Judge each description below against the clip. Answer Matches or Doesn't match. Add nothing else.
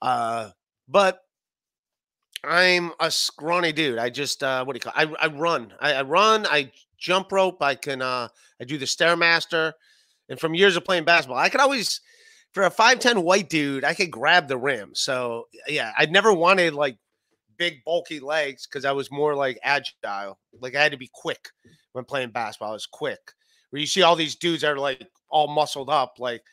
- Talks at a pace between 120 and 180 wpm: Doesn't match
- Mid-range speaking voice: Matches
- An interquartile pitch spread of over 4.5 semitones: Matches